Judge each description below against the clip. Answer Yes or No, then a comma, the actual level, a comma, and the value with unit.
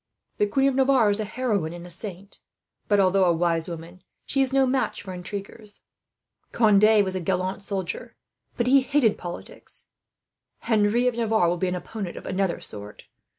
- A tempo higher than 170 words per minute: Yes, average, 180 wpm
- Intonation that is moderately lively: Yes, average, 4.3 semitones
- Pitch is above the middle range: Yes, high, 200 Hz